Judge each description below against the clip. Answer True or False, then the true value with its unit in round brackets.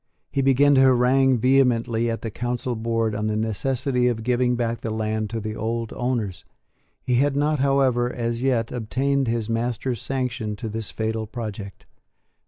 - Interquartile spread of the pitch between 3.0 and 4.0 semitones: False (2.6 semitones)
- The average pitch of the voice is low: True (120 Hz)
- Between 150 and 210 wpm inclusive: True (170 wpm)